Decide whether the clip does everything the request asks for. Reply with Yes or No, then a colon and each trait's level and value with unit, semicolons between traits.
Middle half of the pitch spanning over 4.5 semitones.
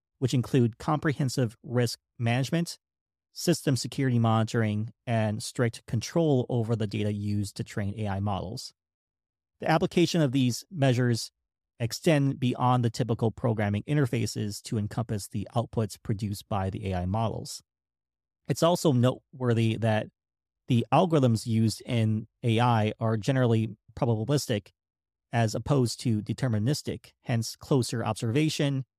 No: average, 3.7 semitones